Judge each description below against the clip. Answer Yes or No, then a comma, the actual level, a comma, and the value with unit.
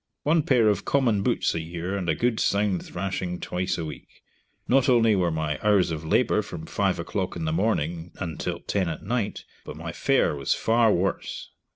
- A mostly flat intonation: No, average, 4.8 semitones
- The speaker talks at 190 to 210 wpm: Yes, average, 195 wpm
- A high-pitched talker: No, very low, 95 Hz